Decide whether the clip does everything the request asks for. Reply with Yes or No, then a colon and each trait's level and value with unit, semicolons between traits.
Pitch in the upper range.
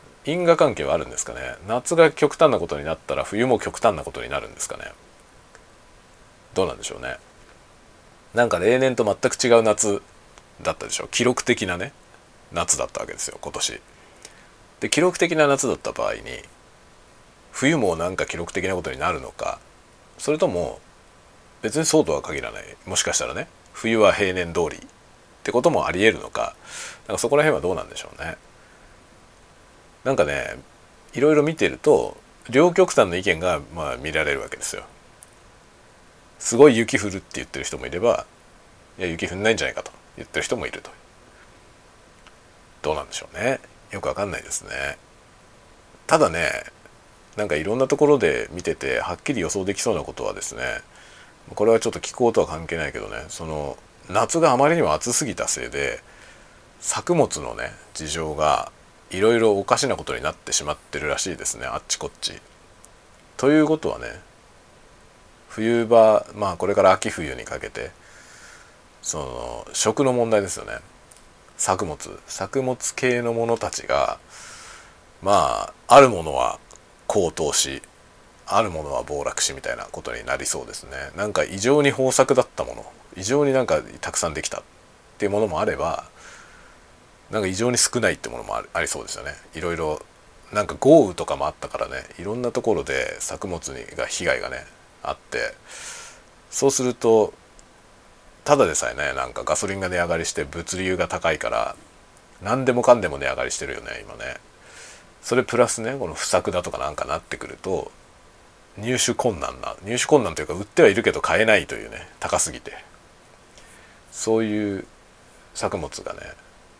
No: low, 115 Hz